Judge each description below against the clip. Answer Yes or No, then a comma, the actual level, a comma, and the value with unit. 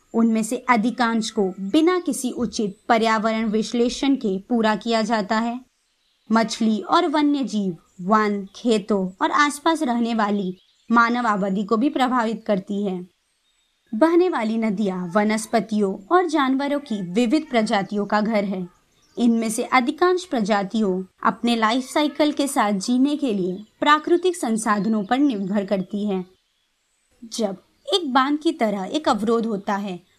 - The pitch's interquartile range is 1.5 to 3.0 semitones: No, average, 3.9 semitones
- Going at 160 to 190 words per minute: No, average, 140 wpm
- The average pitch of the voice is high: Yes, high, 225 Hz